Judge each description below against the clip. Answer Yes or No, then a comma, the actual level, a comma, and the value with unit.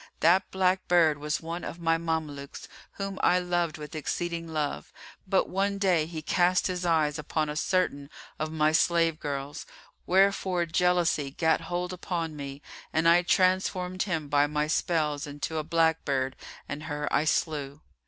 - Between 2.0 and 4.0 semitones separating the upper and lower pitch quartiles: Yes, average, 2.9 semitones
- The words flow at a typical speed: Yes, average, 165 wpm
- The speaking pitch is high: No, medium, 165 Hz